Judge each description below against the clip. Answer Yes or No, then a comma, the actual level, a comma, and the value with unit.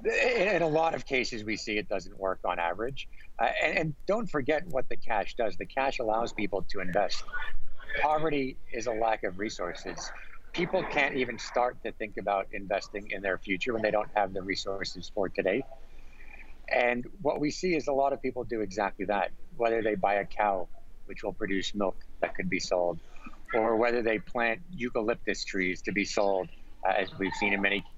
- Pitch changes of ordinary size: No, wide, 6.1 semitones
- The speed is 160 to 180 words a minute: No, average, 195 wpm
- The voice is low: Yes, low, 115 Hz